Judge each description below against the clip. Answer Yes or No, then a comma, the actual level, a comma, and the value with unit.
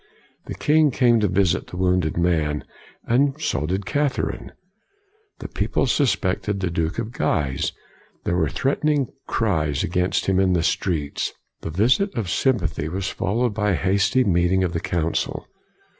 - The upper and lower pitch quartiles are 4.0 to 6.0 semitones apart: Yes, wide, 5.6 semitones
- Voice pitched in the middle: No, very low, 95 Hz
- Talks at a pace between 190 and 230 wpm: No, average, 160 wpm